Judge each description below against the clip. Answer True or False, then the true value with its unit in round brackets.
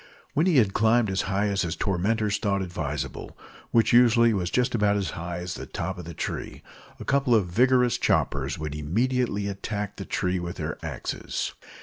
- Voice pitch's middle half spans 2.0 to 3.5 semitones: False (4.8 semitones)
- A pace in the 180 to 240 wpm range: True (185 wpm)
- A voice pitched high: False (100 Hz)